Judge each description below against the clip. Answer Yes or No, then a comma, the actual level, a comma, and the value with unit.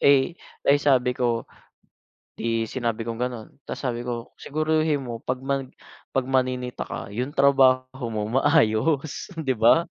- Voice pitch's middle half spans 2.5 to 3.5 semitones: Yes, average, 3.0 semitones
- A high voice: No, low, 130 Hz